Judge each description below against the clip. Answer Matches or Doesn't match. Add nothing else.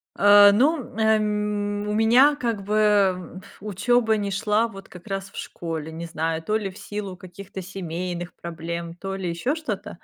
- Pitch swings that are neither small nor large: Matches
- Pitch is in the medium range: Doesn't match